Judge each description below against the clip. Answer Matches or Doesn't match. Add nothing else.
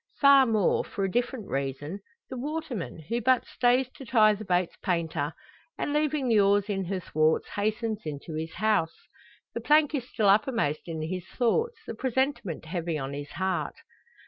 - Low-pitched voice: Doesn't match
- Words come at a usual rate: Matches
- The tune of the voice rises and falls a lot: Matches